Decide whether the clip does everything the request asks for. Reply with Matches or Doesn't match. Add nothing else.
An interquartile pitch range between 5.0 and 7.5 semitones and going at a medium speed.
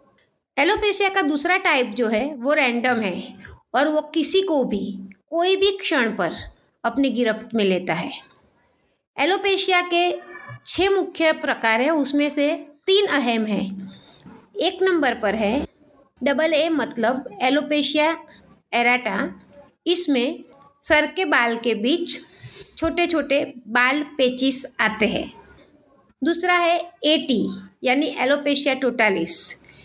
Matches